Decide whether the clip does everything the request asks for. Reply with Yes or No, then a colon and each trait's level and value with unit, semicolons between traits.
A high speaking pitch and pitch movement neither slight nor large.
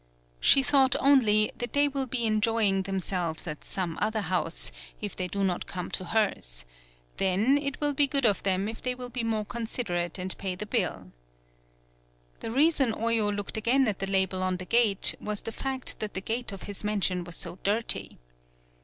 Yes: high, 210 Hz; average, 4.5 semitones